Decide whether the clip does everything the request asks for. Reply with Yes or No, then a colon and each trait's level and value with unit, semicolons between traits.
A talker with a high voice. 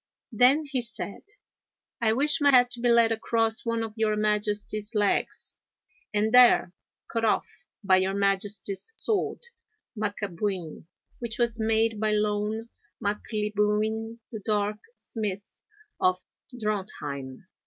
Yes: high, 215 Hz